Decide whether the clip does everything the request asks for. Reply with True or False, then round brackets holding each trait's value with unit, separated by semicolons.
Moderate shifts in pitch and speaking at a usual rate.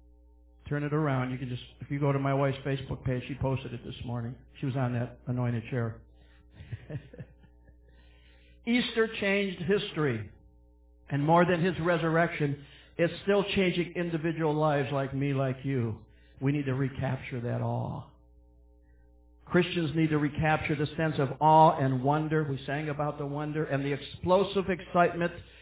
True (4.8 semitones; 155 wpm)